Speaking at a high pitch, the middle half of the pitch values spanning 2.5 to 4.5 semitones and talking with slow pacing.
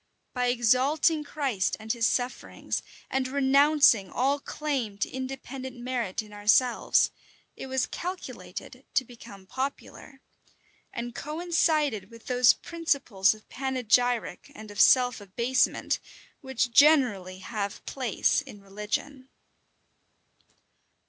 Yes: very high, 250 Hz; average, 4.0 semitones; slow, 110 wpm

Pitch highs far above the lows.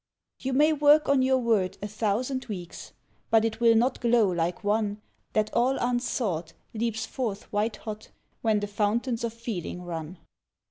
No: average, 3.0 semitones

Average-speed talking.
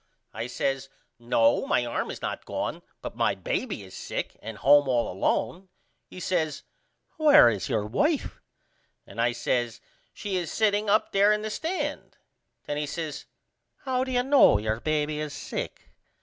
Yes: average, 165 wpm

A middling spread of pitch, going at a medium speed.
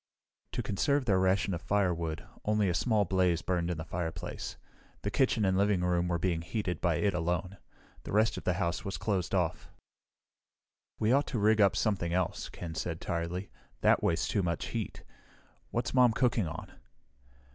Yes: average, 3.3 semitones; average, 180 wpm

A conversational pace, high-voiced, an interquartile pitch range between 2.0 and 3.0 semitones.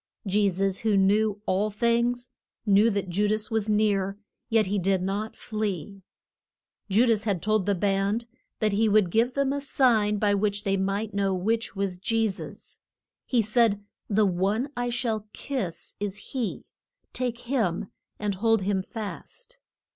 Yes: average, 160 wpm; high, 210 Hz; narrow, 2.5 semitones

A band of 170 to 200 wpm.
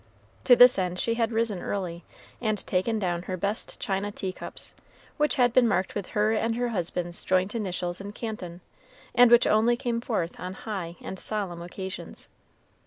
Yes: average, 175 wpm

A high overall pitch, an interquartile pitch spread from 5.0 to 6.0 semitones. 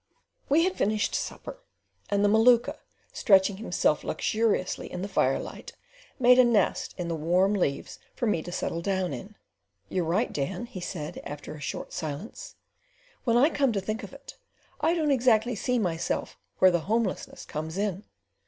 Yes: high, 200 Hz; wide, 5.4 semitones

